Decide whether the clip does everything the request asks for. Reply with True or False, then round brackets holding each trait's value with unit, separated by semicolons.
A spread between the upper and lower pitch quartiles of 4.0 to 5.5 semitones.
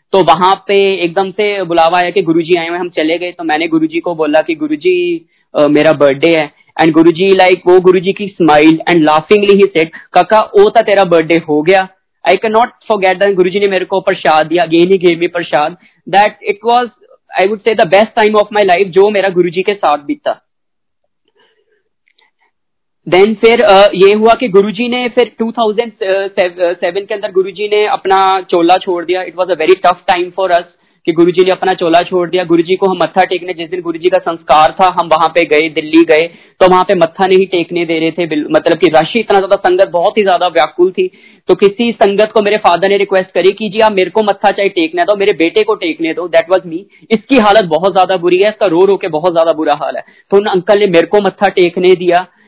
False (3.6 semitones)